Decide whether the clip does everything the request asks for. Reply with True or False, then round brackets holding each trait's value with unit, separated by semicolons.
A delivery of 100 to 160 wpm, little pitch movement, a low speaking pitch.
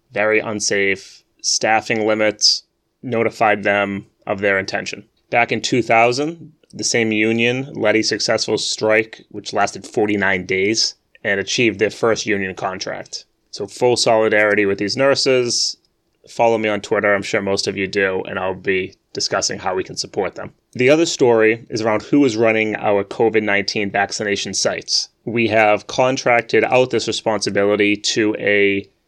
True (155 wpm; 2.2 semitones; 110 Hz)